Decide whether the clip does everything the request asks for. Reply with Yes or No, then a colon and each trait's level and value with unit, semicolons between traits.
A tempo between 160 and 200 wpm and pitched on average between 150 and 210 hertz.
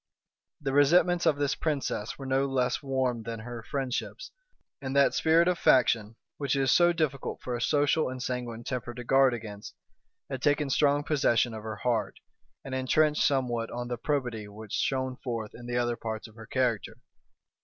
No: average, 185 wpm; low, 130 Hz